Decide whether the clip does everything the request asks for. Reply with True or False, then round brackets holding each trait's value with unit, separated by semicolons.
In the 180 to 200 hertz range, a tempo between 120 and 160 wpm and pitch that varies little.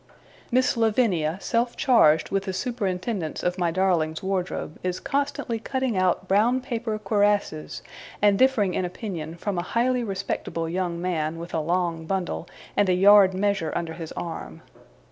False (190 Hz; 155 wpm; 4.4 semitones)